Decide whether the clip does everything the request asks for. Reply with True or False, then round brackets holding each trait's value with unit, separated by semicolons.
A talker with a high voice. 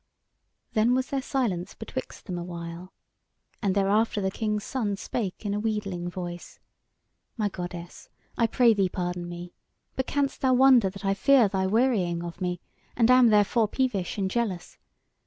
True (200 Hz)